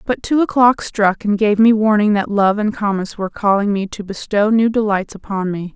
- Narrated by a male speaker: No, female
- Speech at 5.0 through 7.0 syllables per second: Yes, 5.1 syllables/s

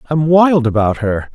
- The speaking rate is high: No, average, 180 wpm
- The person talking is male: Yes, male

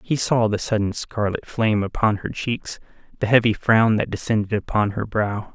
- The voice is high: No, low, 110 Hz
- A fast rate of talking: No, average, 185 wpm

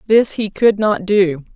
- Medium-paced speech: Yes, average, 195 wpm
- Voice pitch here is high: Yes, high, 200 Hz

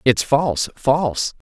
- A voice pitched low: Yes, low, 130 Hz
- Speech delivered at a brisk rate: No, slow, 120 wpm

